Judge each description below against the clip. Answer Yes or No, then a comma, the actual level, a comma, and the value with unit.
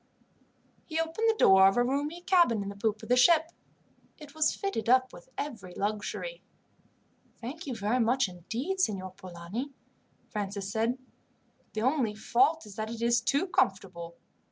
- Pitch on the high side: Yes, high, 235 Hz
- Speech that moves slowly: No, average, 160 wpm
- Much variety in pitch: Yes, wide, 6.9 semitones